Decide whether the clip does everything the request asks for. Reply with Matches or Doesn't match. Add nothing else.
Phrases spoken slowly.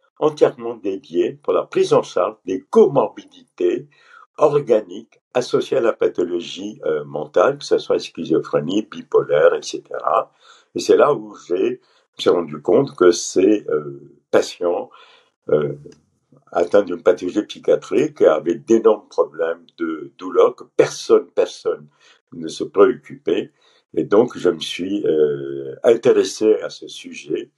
Matches